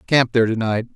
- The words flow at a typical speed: Yes, average, 190 wpm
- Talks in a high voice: No, low, 115 Hz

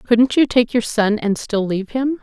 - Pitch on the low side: No, high, 230 Hz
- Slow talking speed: No, fast, 240 wpm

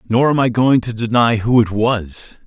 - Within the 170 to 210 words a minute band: No, fast, 220 wpm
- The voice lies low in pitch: Yes, low, 115 Hz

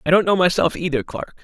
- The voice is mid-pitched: Yes, medium, 170 Hz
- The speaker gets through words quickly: Yes, fast, 250 wpm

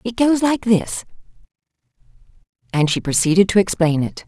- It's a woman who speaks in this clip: Yes, female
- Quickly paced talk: No, average, 140 wpm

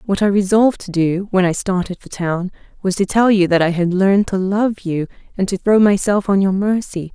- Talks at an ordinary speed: No, fast, 235 wpm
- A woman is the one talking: Yes, female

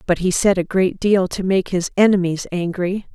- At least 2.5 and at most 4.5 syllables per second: No, 4.9 syllables/s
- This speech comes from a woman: Yes, female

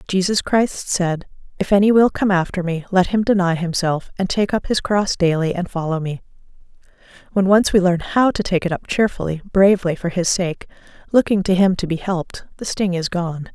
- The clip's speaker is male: No, female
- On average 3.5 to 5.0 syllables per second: No, 5.3 syllables/s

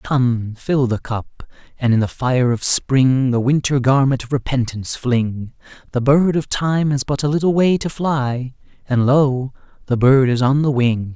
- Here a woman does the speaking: No, male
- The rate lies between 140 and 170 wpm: No, average, 185 wpm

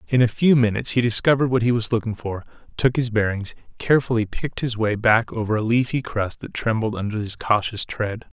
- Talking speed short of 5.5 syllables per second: No, 5.9 syllables/s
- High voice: No, low, 115 Hz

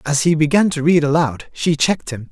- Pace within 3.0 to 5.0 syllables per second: No, 5.5 syllables/s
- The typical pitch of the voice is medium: Yes, medium, 155 Hz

